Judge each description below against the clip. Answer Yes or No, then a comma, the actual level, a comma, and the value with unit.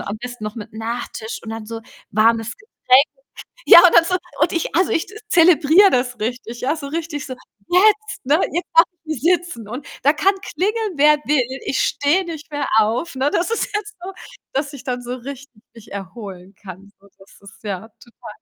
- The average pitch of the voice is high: Yes, very high, 270 Hz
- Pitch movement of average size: No, wide, 6.7 semitones